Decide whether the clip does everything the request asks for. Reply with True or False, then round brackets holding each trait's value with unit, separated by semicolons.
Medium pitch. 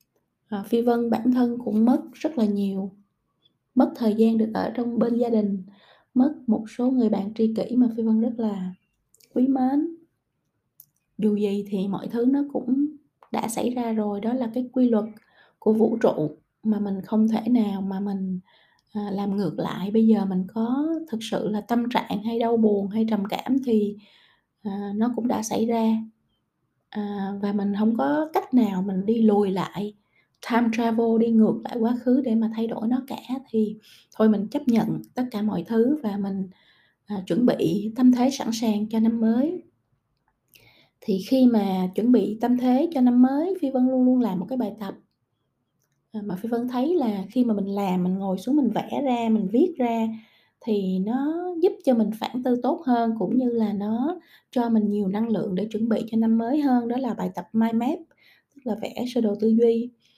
False (225 Hz)